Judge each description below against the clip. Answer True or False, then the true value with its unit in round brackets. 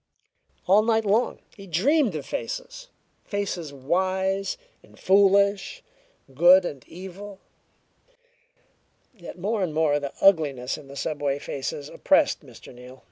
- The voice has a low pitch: False (185 Hz)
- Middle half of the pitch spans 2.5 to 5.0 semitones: False (5.6 semitones)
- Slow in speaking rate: True (125 wpm)